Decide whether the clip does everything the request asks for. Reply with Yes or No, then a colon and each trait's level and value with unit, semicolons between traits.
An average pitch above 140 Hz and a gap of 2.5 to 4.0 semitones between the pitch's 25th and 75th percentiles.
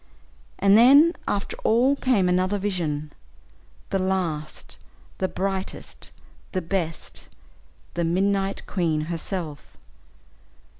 Yes: high, 190 Hz; average, 3.1 semitones